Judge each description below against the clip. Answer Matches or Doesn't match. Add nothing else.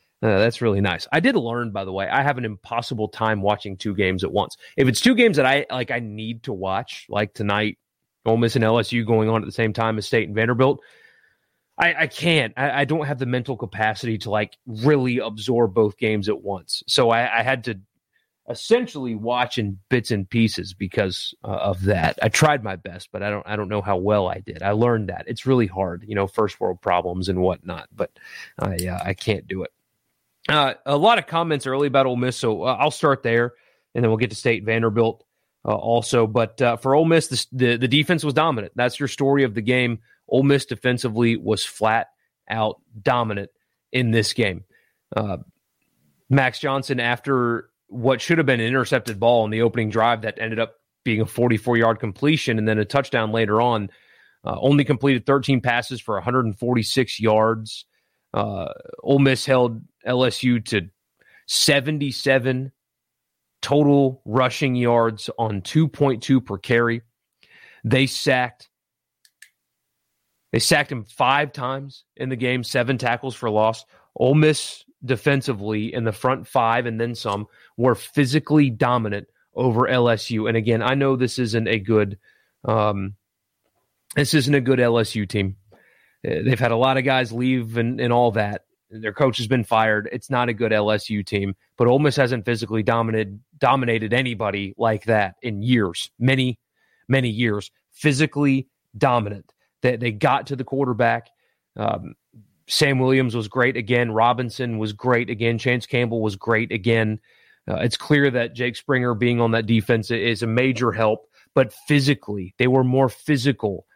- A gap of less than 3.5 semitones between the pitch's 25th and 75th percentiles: Matches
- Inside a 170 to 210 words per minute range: Matches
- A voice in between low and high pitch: Doesn't match